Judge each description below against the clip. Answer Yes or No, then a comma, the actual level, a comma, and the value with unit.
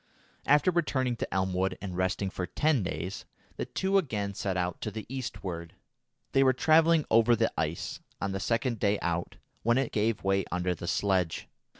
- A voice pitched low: Yes, low, 100 Hz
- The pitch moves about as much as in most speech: No, wide, 5.9 semitones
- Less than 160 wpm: No, average, 180 wpm